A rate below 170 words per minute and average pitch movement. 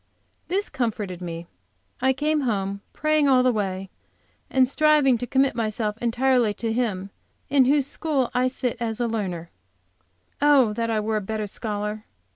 Yes: average, 155 wpm; average, 4.1 semitones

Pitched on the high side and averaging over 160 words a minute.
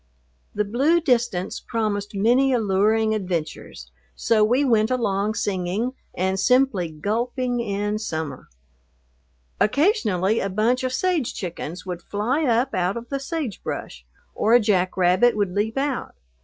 No: high, 215 Hz; slow, 135 wpm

